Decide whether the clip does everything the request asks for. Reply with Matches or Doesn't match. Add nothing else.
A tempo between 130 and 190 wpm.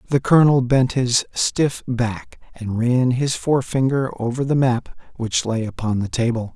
Matches